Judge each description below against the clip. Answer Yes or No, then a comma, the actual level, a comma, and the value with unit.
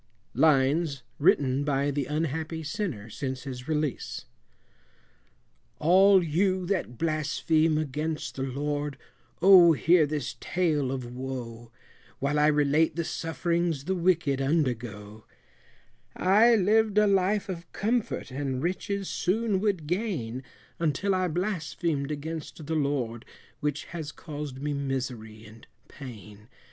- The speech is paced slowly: Yes, slow, 120 wpm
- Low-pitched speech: No, medium, 150 Hz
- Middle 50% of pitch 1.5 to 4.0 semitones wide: No, average, 4.7 semitones